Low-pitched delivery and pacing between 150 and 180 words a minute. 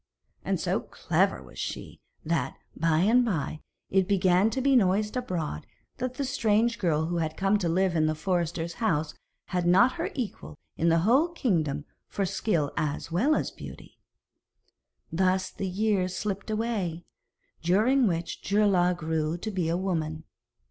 No: medium, 185 Hz; average, 160 wpm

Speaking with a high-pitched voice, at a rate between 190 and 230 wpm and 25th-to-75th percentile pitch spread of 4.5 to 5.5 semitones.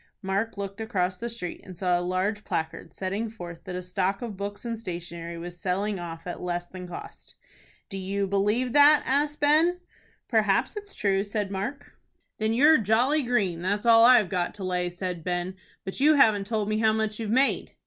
No: high, 200 Hz; average, 195 wpm; average, 4.0 semitones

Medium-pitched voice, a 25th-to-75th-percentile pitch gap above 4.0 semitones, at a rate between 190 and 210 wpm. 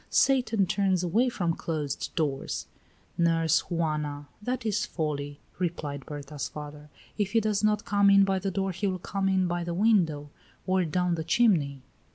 No: medium, 175 Hz; average, 4.7 semitones; average, 170 wpm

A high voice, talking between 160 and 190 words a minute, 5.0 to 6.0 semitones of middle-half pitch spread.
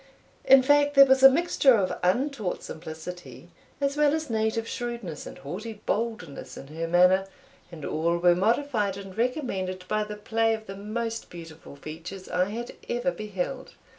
Yes: high, 210 Hz; average, 165 wpm; wide, 5.4 semitones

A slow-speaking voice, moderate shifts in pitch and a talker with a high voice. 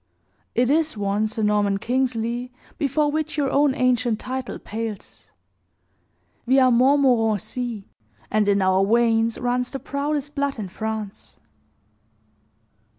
Yes: slow, 120 wpm; average, 3.8 semitones; high, 240 Hz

